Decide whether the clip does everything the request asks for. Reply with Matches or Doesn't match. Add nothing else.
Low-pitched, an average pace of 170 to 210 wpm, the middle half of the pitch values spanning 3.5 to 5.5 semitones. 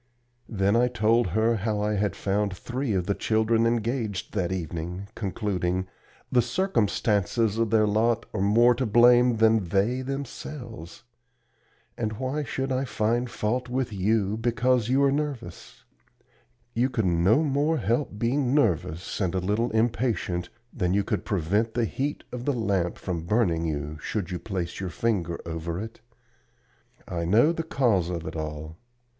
Doesn't match